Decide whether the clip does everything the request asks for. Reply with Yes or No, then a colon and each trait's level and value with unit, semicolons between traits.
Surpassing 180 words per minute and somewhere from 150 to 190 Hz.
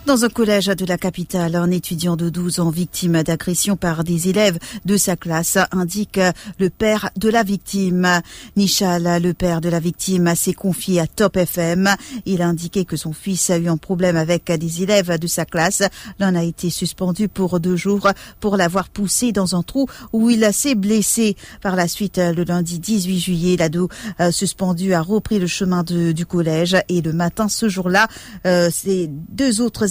Yes: average, 190 wpm; medium, 185 Hz